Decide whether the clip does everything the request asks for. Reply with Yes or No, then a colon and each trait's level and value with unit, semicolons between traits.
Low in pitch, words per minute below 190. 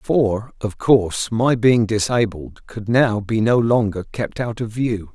Yes: low, 110 Hz; average, 175 wpm